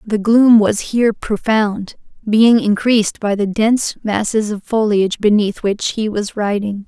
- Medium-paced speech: Yes, average, 155 wpm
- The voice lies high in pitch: Yes, high, 215 Hz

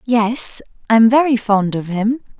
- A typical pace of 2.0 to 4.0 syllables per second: Yes, 3.8 syllables/s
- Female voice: Yes, female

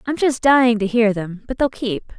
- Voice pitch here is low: No, high, 230 Hz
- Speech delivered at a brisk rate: Yes, fast, 245 wpm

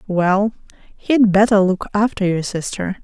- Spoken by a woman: Yes, female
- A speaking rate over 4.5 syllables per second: No, 4.1 syllables/s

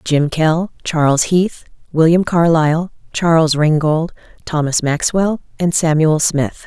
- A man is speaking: No, female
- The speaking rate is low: Yes, slow, 115 wpm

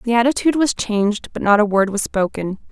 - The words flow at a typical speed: No, fast, 220 wpm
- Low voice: No, high, 220 Hz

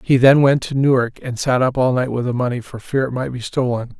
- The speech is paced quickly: Yes, fast, 285 wpm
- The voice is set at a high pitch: No, low, 125 Hz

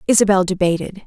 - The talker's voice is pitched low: No, high, 190 Hz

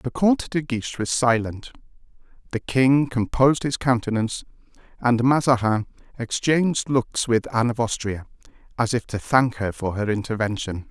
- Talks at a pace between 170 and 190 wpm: No, average, 150 wpm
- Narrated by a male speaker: Yes, male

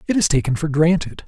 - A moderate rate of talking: No, fast, 235 wpm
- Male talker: Yes, male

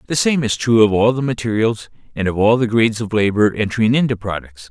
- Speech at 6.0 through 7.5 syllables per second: Yes, 6.1 syllables/s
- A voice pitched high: No, low, 110 Hz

